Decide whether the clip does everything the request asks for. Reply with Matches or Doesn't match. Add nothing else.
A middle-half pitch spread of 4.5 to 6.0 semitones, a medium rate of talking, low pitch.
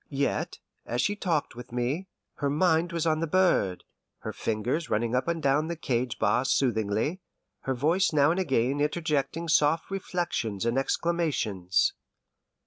Doesn't match